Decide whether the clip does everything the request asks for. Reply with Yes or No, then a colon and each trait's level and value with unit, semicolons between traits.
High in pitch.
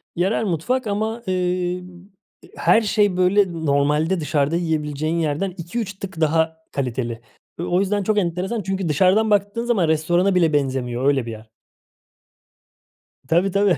No: medium, 180 Hz